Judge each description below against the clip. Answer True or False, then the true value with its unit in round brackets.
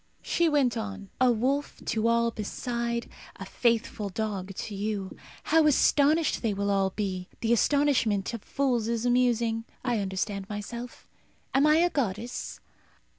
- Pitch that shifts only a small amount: False (3.7 semitones)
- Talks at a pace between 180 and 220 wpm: False (145 wpm)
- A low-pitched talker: False (230 Hz)